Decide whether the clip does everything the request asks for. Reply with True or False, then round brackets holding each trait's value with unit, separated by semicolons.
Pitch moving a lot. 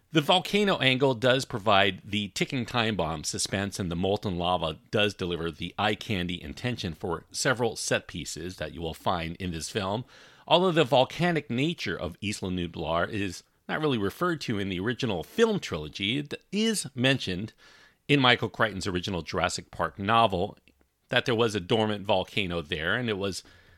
True (6.1 semitones)